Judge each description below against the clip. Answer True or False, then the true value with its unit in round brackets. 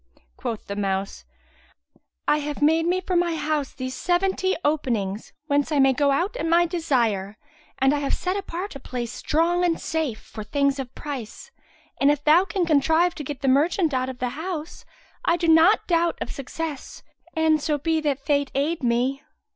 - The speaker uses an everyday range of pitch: True (4.1 semitones)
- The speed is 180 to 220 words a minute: True (185 wpm)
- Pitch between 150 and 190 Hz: False (295 Hz)